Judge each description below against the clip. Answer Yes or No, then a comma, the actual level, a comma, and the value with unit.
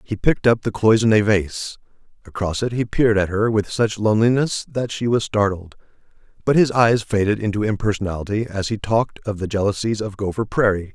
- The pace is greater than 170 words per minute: Yes, average, 185 wpm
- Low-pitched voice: Yes, low, 105 Hz